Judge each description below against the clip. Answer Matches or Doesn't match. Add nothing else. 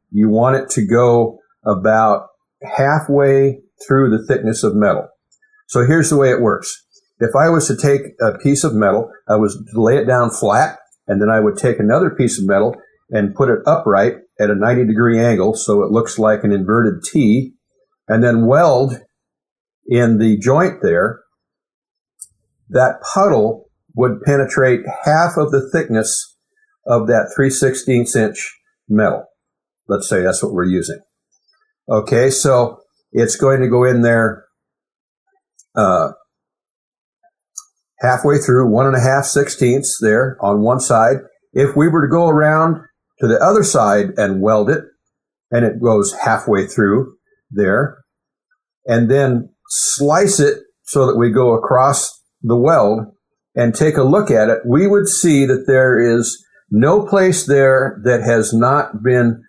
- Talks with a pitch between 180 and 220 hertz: Doesn't match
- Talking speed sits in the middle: Matches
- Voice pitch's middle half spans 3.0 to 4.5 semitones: Doesn't match